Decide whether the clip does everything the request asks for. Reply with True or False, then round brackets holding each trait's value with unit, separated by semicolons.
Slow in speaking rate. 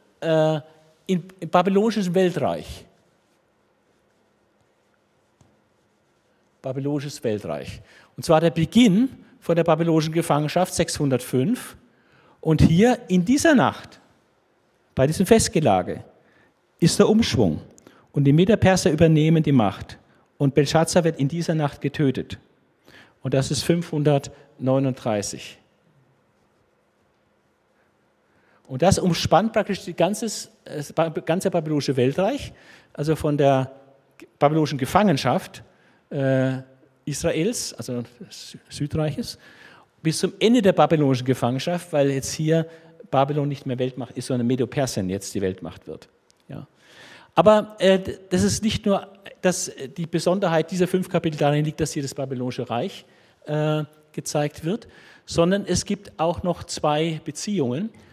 True (110 wpm)